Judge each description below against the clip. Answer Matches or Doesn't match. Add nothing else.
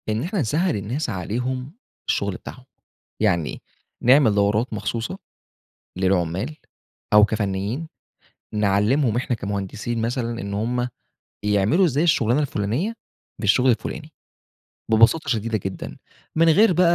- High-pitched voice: Doesn't match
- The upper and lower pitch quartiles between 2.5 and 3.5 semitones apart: Doesn't match